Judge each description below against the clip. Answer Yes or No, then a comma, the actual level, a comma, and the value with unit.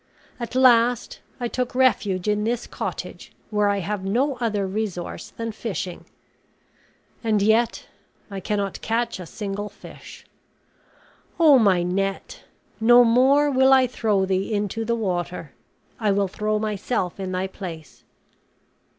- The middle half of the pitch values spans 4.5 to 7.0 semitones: No, average, 3.5 semitones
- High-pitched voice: Yes, high, 210 Hz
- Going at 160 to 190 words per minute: No, slow, 135 wpm